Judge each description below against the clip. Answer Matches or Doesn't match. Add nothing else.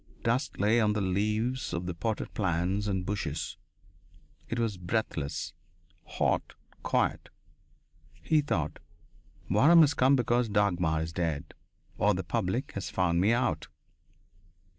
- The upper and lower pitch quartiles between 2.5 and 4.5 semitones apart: Doesn't match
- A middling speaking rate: Doesn't match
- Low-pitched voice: Matches